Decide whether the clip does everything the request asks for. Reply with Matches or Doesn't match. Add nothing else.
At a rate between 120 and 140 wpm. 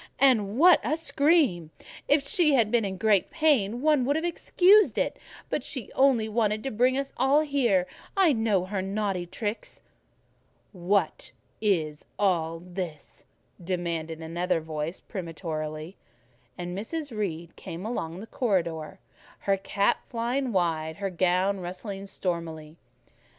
Matches